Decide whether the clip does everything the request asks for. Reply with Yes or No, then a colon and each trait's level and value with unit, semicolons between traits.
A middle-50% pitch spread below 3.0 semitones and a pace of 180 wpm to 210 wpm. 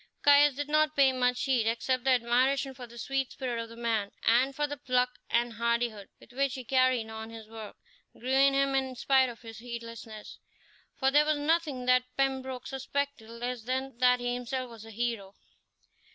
Yes: narrow, 2.5 semitones; average, 195 wpm